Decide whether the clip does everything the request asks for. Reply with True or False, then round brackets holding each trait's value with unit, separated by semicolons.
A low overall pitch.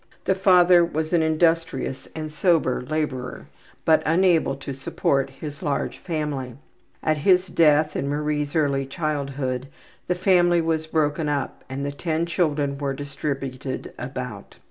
False (150 Hz)